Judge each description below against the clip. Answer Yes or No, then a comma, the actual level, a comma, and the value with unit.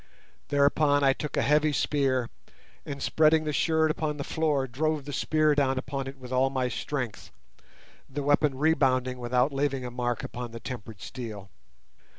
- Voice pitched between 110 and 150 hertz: Yes, low, 135 Hz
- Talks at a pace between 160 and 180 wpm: Yes, average, 165 wpm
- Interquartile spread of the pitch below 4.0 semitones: Yes, average, 2.8 semitones